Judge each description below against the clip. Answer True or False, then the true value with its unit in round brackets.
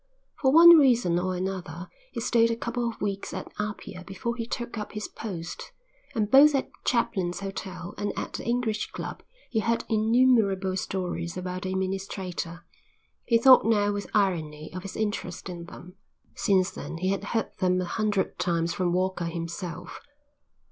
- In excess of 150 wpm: True (170 wpm)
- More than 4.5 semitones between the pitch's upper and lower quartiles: False (4.0 semitones)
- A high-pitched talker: True (195 Hz)